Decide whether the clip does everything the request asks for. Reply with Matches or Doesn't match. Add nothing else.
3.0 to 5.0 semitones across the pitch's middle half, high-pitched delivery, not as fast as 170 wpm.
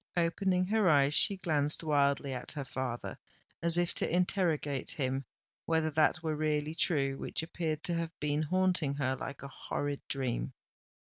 Doesn't match